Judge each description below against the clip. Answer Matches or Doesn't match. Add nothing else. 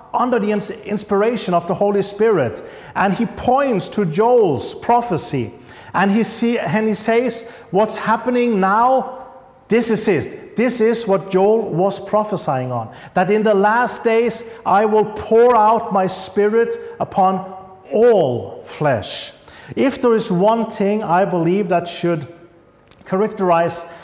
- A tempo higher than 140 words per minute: Doesn't match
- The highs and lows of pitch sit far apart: Doesn't match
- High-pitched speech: Matches